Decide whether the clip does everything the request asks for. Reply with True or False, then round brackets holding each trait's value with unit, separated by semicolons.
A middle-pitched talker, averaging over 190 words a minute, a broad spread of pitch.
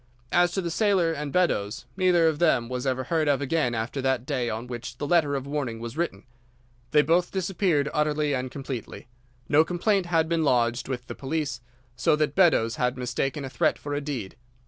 False (145 Hz; 200 wpm; 4.6 semitones)